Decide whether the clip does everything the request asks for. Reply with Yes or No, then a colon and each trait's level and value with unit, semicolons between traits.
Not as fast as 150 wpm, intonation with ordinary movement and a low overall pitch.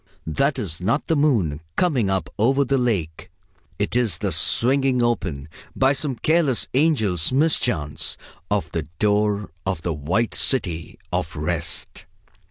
No: average, 140 wpm; wide, 7.5 semitones; low, 110 Hz